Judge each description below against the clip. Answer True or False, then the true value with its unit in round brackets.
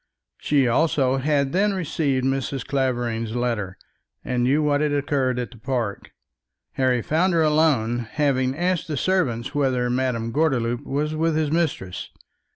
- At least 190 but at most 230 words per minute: False (150 wpm)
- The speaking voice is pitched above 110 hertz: True (135 Hz)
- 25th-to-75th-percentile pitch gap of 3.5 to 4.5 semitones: True (3.9 semitones)